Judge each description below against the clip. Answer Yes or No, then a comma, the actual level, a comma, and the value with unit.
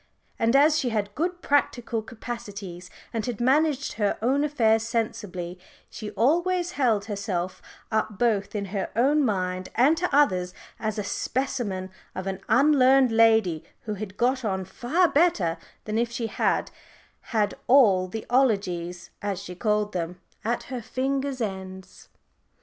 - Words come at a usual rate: Yes, average, 150 wpm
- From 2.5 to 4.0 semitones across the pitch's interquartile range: No, average, 5.1 semitones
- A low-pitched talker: No, high, 225 Hz